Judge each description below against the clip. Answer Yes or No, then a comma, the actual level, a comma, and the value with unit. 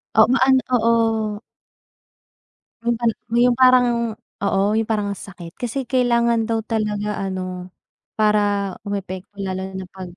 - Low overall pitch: No, high, 215 Hz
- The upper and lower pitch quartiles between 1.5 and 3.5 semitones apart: Yes, average, 3.2 semitones